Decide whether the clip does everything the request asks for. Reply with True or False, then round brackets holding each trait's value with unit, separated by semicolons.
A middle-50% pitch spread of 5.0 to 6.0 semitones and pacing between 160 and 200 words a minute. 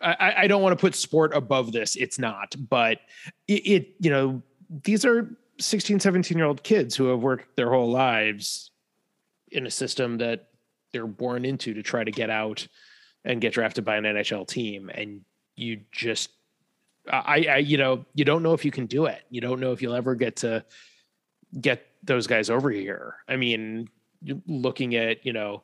True (5.4 semitones; 190 wpm)